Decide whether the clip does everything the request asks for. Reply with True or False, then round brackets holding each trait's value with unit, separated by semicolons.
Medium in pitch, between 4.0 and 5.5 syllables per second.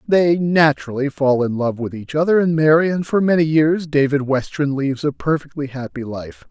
True (145 Hz; 5.0 syllables/s)